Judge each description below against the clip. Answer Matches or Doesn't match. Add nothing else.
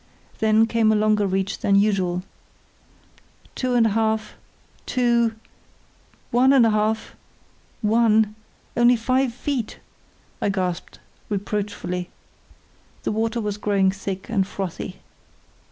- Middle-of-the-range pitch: Doesn't match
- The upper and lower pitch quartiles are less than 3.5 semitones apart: Matches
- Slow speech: Matches